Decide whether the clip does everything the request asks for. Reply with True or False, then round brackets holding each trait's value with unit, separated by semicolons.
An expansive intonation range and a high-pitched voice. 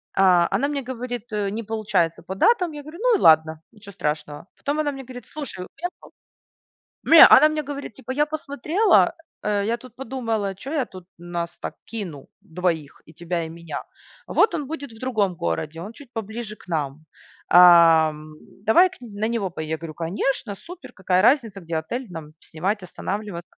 True (7.8 semitones; 210 Hz)